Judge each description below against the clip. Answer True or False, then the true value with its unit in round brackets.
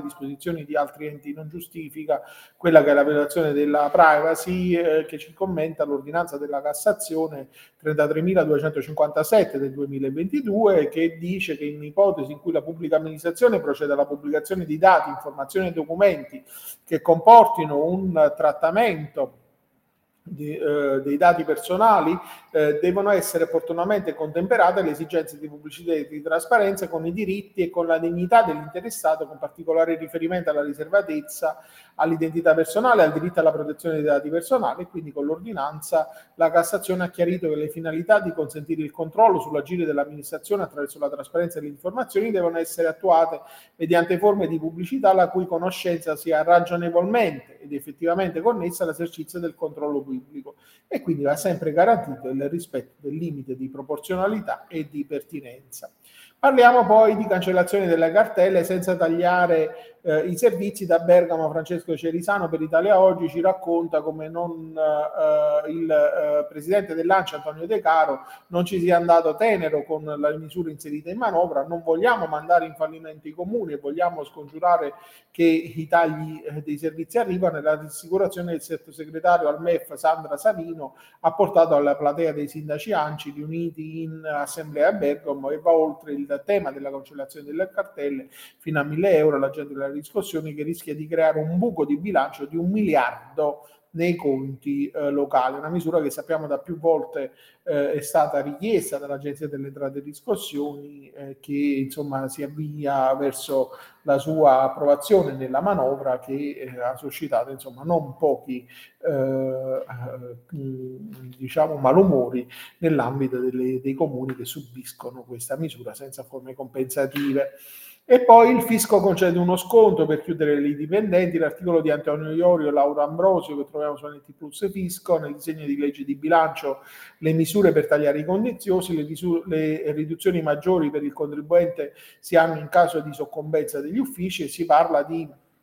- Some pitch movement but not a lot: True (3.4 semitones)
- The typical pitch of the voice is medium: True (160 Hz)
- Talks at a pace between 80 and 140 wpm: False (155 wpm)